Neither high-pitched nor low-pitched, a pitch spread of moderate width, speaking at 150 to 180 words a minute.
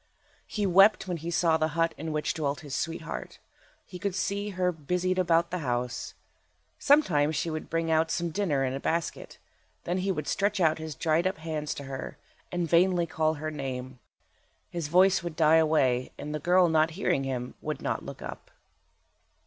No: medium, 165 Hz; average, 3.1 semitones; average, 190 wpm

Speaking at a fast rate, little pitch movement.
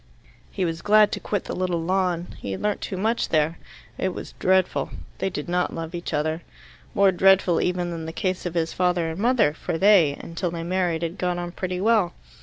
Yes: fast, 210 wpm; narrow, 2.2 semitones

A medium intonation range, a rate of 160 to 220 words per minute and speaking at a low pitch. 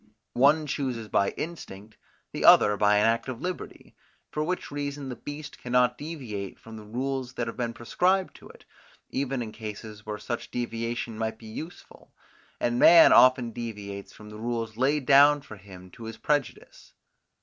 Yes: average, 4.3 semitones; average, 170 wpm; low, 120 Hz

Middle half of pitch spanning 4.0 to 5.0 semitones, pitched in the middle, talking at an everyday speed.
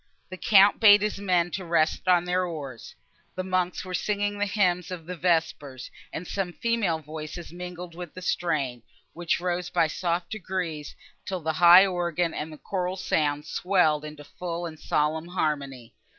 No: average, 2.7 semitones; medium, 175 Hz; average, 165 wpm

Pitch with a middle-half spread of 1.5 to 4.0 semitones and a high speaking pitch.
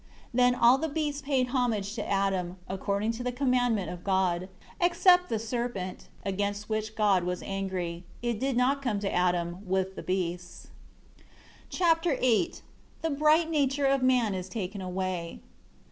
No: wide, 5.6 semitones; high, 215 Hz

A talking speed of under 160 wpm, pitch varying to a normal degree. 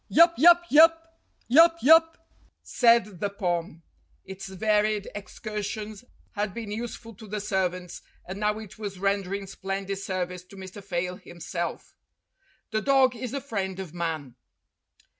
Yes: average, 140 wpm; average, 3.6 semitones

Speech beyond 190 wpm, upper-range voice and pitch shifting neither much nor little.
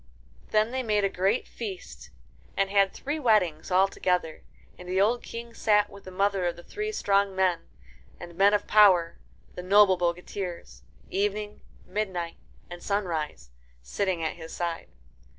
No: average, 155 wpm; high, 195 Hz; average, 3.0 semitones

